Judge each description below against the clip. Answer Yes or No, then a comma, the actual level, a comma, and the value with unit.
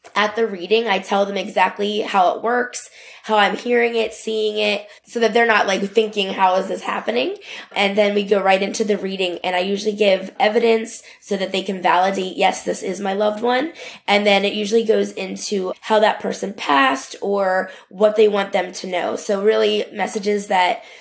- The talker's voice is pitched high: Yes, high, 205 Hz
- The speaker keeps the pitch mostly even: Yes, narrow, 2.3 semitones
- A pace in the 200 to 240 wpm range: Yes, fast, 205 wpm